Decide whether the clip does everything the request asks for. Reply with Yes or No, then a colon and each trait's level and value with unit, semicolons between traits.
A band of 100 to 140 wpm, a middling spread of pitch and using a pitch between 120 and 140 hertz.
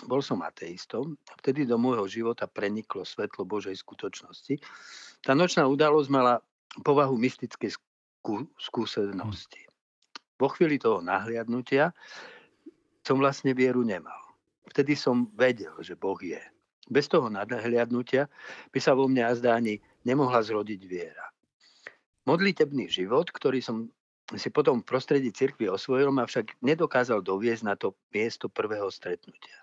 Yes: average, 130 wpm; average, 3.2 semitones; low, 125 Hz